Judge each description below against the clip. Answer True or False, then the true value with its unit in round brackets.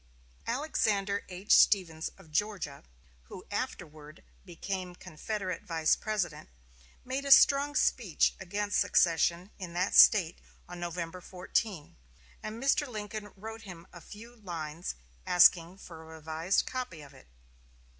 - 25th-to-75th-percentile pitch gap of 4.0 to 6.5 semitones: True (4.4 semitones)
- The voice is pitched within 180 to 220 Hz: True (185 Hz)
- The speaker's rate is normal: False (125 wpm)